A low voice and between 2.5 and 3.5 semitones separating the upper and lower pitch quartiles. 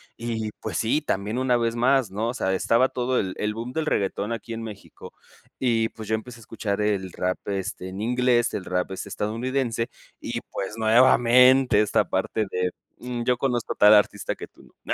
Yes: low, 115 Hz; average, 3.1 semitones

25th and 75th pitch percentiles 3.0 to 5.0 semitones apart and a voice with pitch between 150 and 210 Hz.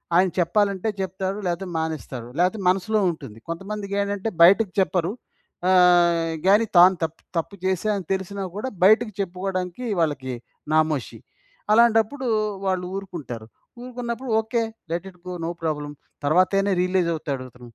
Yes: average, 3.5 semitones; medium, 185 Hz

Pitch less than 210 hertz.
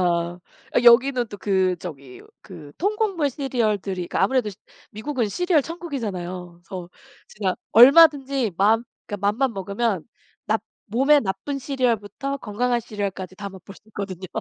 No: high, 215 Hz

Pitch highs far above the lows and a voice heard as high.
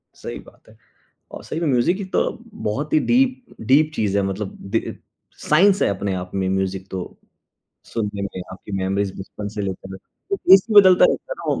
No: wide, 9.0 semitones; low, 105 Hz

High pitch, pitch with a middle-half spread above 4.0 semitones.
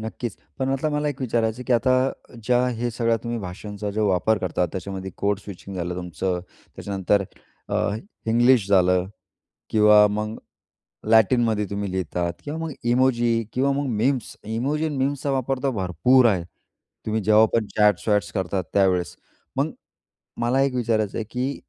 No: low, 110 Hz; average, 4.5 semitones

